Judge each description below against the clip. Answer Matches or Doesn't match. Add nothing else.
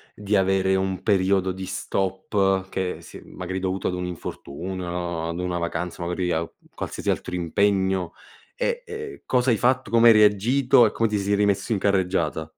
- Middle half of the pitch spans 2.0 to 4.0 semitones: Matches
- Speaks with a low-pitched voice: Matches